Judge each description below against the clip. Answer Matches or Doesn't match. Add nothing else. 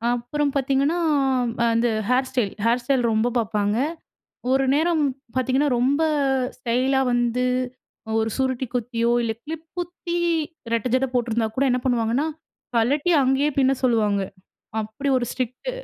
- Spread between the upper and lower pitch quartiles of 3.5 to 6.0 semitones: Doesn't match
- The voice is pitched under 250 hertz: Doesn't match